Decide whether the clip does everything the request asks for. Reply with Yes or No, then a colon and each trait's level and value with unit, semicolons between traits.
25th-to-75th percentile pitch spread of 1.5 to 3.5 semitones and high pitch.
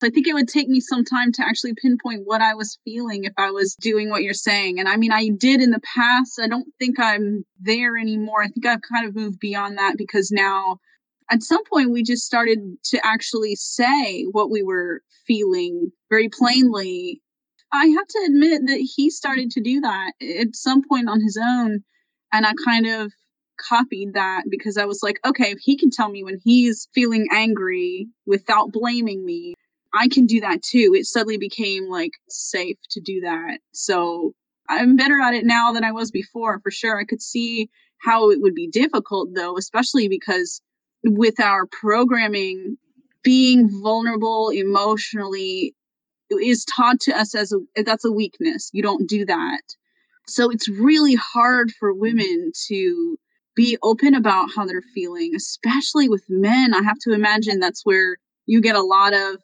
No: average, 4.0 semitones; high, 230 Hz